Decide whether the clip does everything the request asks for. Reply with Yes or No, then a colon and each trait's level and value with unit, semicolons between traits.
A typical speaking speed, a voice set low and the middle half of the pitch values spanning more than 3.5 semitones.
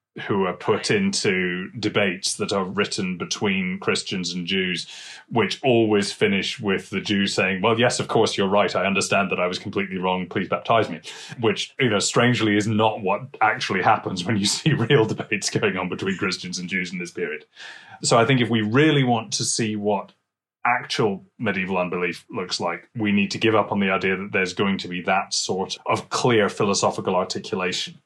Yes: average, 195 wpm; low, 105 Hz; average, 4.9 semitones